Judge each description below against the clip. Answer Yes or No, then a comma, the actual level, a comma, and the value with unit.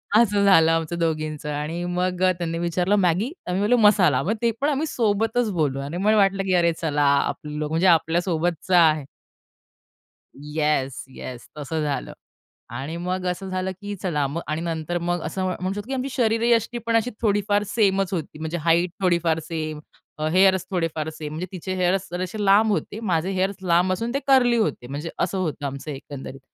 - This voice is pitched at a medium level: Yes, medium, 180 Hz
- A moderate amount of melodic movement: Yes, average, 4.1 semitones